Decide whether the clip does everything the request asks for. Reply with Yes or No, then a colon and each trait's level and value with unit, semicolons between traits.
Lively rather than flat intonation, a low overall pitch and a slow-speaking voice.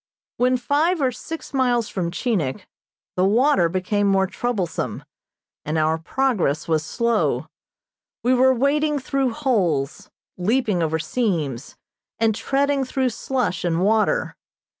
No: wide, 7.0 semitones; high, 225 Hz; slow, 125 wpm